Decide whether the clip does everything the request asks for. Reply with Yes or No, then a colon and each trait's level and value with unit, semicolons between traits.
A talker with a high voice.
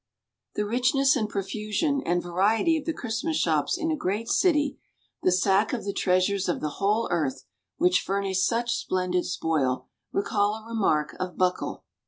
Yes: high, 200 Hz